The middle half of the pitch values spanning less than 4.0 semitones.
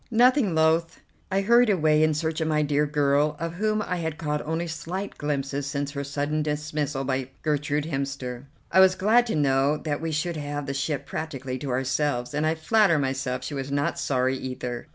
Yes: average, 2.8 semitones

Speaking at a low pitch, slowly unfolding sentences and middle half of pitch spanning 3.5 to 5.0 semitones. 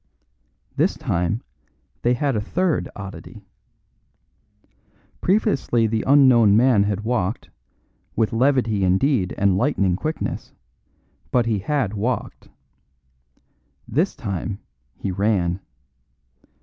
Yes: low, 110 Hz; slow, 95 wpm; average, 4.6 semitones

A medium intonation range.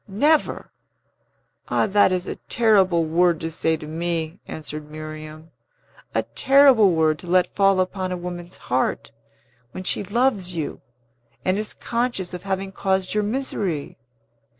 Yes: average, 3.9 semitones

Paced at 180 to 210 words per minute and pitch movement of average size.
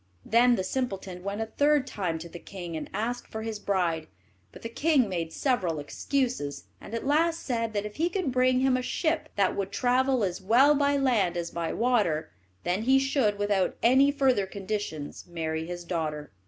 No: average, 195 wpm; wide, 6.6 semitones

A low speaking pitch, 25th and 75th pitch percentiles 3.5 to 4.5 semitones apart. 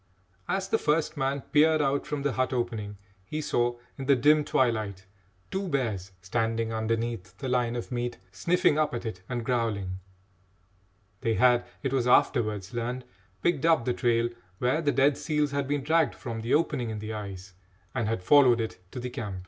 Yes: low, 120 Hz; average, 4.1 semitones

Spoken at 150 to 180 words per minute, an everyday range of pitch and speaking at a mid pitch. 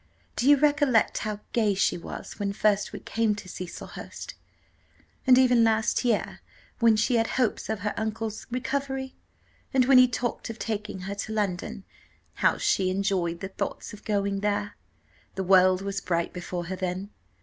No: average, 170 wpm; average, 3.4 semitones; high, 210 Hz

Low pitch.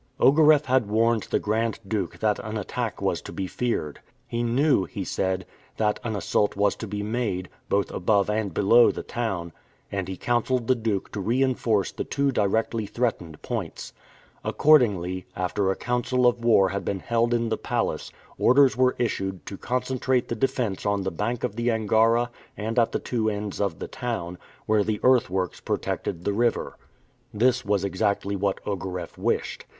Yes: low, 110 Hz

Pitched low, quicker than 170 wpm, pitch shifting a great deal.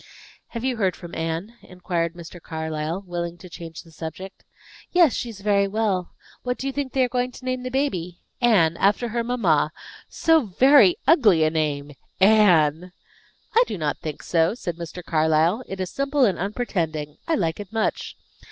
No: medium, 185 Hz; average, 180 wpm; wide, 6.6 semitones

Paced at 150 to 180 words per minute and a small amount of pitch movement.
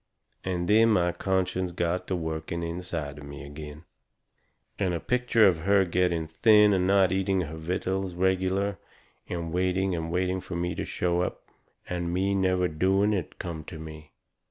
Yes: average, 170 wpm; narrow, 2.2 semitones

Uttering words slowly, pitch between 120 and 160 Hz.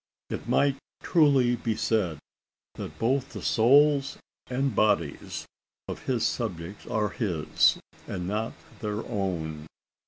No: slow, 120 wpm; low, 110 Hz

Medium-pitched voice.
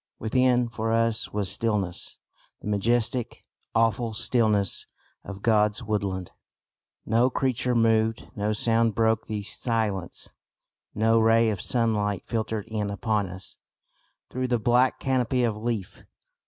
No: low, 110 Hz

